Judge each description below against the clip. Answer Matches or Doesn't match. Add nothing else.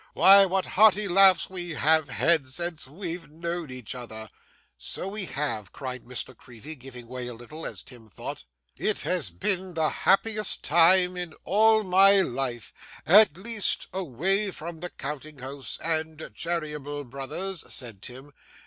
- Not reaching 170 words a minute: Matches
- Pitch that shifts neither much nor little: Doesn't match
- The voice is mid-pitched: Matches